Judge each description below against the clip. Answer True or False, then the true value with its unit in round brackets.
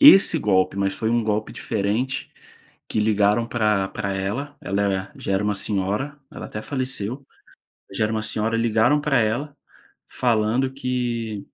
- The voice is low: True (110 Hz)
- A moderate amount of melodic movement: True (3.8 semitones)